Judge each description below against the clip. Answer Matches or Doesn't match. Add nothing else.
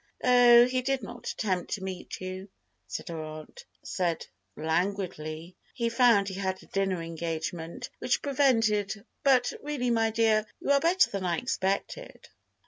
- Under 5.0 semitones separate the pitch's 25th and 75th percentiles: Doesn't match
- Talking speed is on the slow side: Doesn't match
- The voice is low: Doesn't match